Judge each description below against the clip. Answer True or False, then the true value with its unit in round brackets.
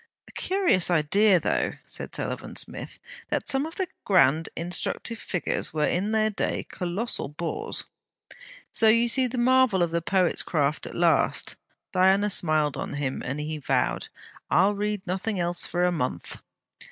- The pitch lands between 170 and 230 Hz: True (185 Hz)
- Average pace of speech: True (160 wpm)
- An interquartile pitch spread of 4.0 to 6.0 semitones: True (5.1 semitones)